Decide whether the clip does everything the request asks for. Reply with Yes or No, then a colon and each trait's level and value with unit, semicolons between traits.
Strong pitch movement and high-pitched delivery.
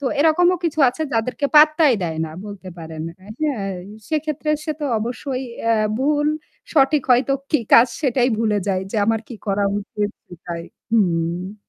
Yes: wide, 6.6 semitones; high, 230 Hz